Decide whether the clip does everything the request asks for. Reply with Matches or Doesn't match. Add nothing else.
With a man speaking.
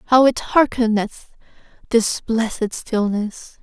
Doesn't match